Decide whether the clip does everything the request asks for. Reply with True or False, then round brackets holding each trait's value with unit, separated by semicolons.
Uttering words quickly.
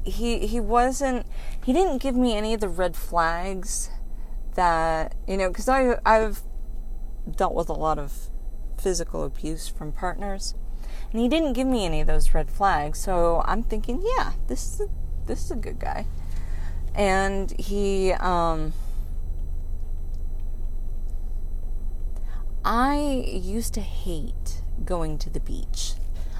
False (135 wpm)